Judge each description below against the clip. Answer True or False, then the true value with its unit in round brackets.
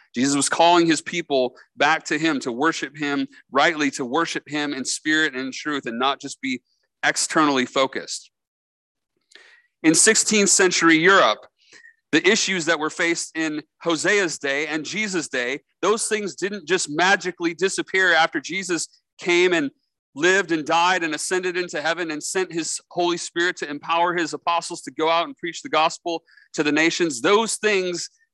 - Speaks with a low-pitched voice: False (170 Hz)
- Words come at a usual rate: True (165 wpm)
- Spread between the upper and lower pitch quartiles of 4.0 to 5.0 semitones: False (3.4 semitones)